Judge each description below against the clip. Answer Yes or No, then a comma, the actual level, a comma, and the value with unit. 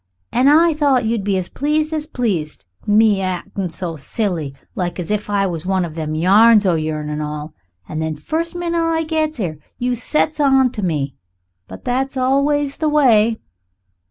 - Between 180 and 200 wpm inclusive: Yes, average, 185 wpm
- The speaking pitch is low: No, high, 215 Hz